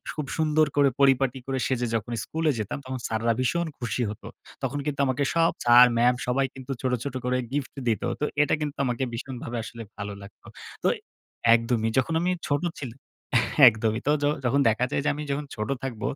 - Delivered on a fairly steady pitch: No, average, 3.5 semitones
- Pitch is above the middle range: No, low, 130 Hz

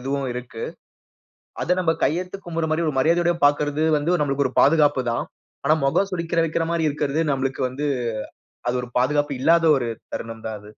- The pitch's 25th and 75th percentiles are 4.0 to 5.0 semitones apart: No, average, 3.6 semitones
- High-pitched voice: No, medium, 145 Hz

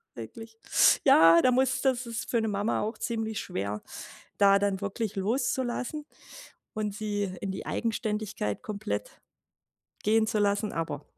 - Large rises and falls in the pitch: No, narrow, 2.6 semitones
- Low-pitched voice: No, high, 215 Hz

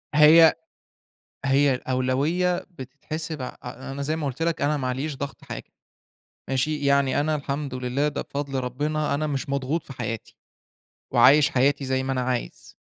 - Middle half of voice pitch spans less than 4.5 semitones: Yes, narrow, 2.6 semitones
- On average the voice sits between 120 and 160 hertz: Yes, medium, 140 Hz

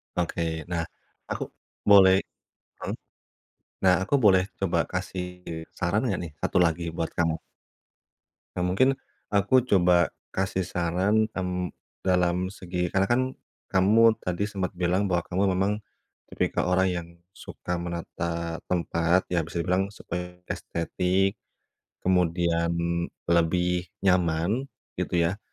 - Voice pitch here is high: No, very low, 90 Hz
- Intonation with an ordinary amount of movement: No, narrow, 1.9 semitones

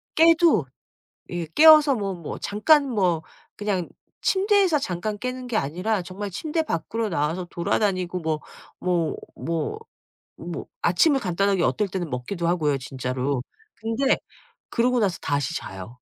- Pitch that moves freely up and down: Yes, wide, 7.1 semitones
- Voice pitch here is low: No, high, 190 Hz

